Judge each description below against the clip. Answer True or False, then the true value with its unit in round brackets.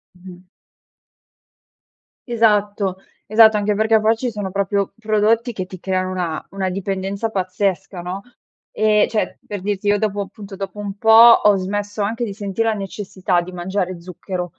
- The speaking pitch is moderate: False (200 Hz)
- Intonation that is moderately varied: False (2.2 semitones)